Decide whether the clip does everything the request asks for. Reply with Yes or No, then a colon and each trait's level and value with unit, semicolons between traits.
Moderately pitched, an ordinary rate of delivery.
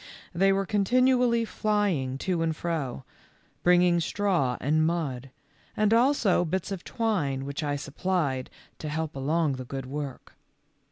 Yes: medium, 165 Hz; average, 145 wpm